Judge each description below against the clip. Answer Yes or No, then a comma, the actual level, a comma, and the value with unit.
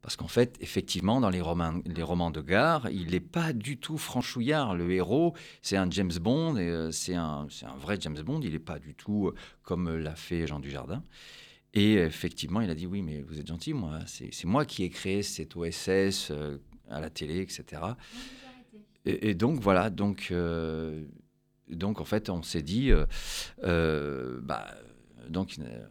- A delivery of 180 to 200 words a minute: Yes, average, 190 wpm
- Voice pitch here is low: Yes, very low, 90 Hz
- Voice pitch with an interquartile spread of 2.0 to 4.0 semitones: No, average, 4.9 semitones